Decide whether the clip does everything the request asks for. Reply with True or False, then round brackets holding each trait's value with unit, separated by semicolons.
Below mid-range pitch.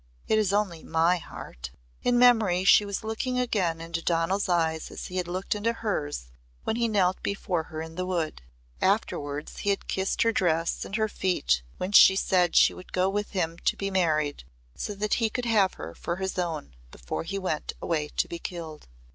False (185 Hz)